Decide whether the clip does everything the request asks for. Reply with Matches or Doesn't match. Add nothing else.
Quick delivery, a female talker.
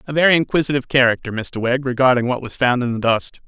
Doesn't match